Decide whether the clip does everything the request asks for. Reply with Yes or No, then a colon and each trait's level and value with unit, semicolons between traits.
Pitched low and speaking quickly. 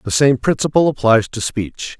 No: low, 120 Hz; average, 180 wpm